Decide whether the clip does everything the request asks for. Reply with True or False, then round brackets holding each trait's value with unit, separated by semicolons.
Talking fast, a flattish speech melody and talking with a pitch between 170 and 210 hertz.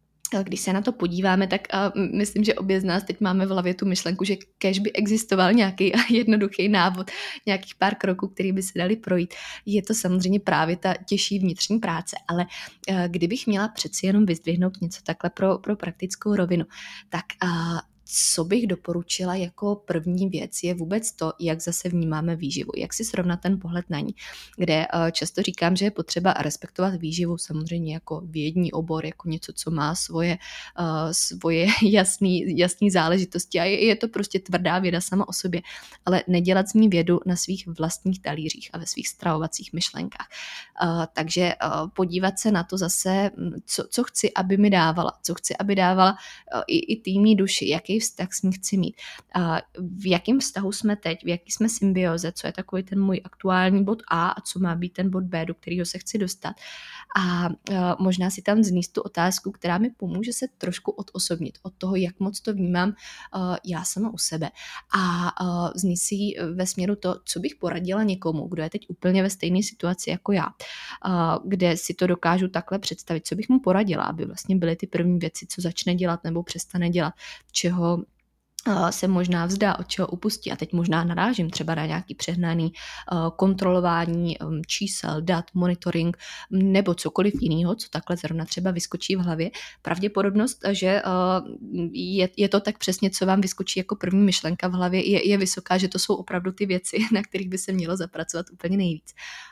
True (180 wpm; 2.3 semitones; 185 Hz)